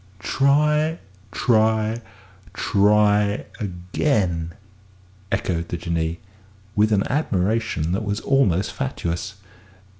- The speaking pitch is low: Yes, low, 105 Hz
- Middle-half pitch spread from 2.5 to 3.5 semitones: No, average, 4.4 semitones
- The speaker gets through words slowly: Yes, slow, 85 wpm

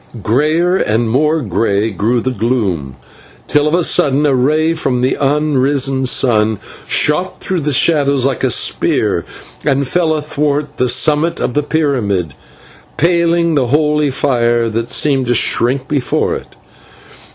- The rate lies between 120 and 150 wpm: Yes, average, 145 wpm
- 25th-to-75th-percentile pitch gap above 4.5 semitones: No, average, 4.0 semitones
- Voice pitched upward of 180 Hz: No, medium, 140 Hz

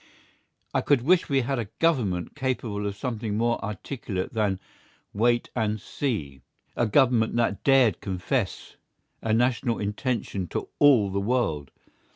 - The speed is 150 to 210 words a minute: No, average, 140 wpm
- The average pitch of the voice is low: Yes, low, 115 Hz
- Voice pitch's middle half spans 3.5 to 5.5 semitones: Yes, average, 4.1 semitones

